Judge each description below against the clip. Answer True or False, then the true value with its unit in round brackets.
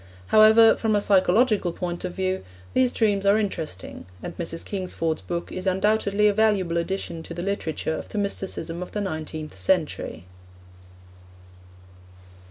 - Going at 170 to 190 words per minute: False (145 wpm)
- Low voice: False (190 Hz)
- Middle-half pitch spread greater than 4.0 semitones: False (3.6 semitones)